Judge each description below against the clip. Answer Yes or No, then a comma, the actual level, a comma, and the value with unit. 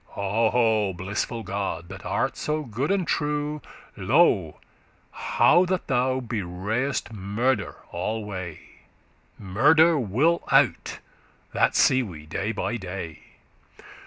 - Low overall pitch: Yes, low, 110 Hz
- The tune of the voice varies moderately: No, wide, 5.9 semitones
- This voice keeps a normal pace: No, slow, 105 wpm